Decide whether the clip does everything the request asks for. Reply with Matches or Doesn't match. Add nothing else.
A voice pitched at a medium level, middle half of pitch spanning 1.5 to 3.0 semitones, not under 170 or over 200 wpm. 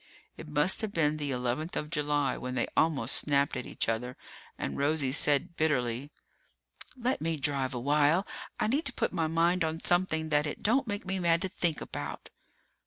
Doesn't match